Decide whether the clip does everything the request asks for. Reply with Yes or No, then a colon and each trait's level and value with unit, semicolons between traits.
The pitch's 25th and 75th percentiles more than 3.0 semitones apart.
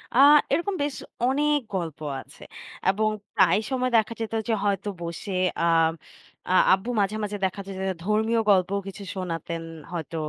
Yes: average, 3.6 semitones